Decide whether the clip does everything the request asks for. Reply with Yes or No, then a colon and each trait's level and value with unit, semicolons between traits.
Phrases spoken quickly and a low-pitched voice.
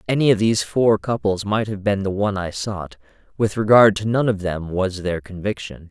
Yes: fast, 215 wpm; low, 100 Hz